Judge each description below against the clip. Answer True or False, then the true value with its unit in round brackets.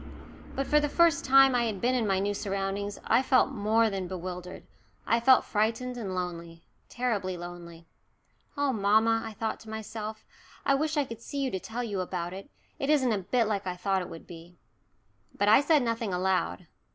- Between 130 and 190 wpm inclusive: False (205 wpm)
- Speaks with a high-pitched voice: True (215 Hz)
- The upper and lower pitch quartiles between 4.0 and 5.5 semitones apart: True (5.0 semitones)